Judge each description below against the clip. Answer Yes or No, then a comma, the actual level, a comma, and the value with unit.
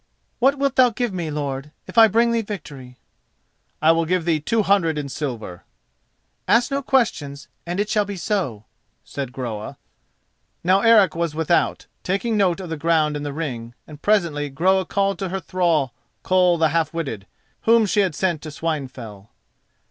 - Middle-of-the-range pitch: Yes, medium, 170 Hz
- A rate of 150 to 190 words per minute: Yes, average, 180 wpm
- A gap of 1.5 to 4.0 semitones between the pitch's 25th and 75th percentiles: No, wide, 5.5 semitones